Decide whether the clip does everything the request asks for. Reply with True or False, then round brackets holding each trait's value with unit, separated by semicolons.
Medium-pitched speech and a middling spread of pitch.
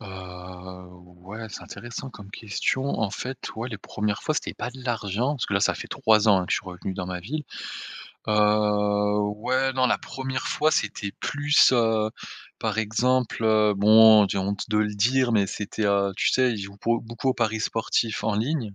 False (110 Hz; 3.2 semitones)